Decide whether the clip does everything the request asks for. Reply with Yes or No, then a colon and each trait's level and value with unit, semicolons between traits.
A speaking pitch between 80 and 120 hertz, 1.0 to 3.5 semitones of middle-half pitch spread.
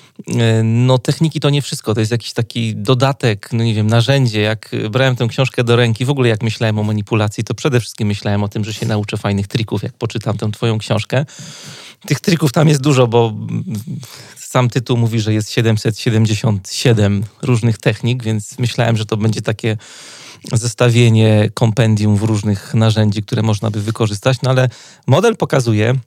Yes: low, 115 Hz; average, 2.8 semitones